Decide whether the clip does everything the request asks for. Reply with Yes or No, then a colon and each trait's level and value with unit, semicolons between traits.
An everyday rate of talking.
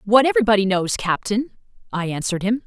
Yes: average, 160 wpm